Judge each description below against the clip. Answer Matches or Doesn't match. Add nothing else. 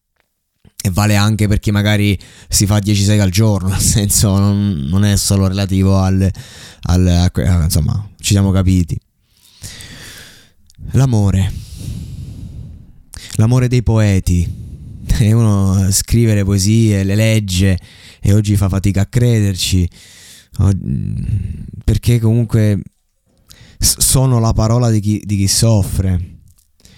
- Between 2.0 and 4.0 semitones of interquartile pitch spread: Matches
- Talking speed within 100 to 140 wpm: Matches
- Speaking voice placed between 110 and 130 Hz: Doesn't match